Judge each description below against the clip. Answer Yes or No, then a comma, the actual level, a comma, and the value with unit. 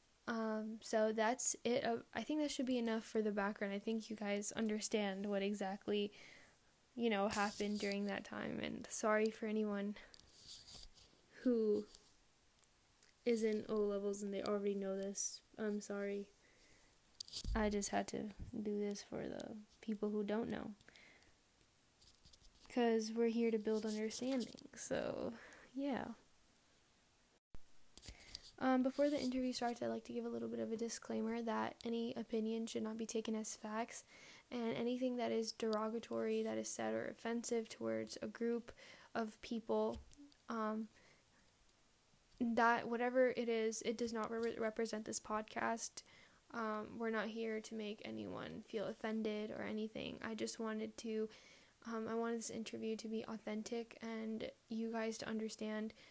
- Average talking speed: Yes, average, 150 wpm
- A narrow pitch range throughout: Yes, narrow, 1.8 semitones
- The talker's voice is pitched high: Yes, high, 220 Hz